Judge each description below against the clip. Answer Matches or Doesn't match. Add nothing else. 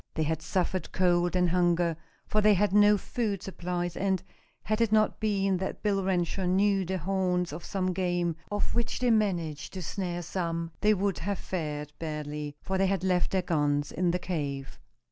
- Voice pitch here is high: Doesn't match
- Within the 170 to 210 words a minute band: Matches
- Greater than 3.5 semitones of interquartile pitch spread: Doesn't match